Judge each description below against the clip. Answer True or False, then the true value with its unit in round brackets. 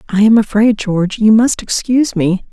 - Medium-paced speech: True (190 wpm)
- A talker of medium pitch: False (215 Hz)